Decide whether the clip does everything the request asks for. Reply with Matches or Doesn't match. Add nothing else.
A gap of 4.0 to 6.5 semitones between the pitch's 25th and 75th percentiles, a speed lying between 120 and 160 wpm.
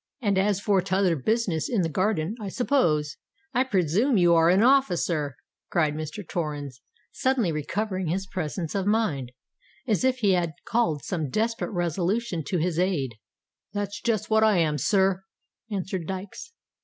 Matches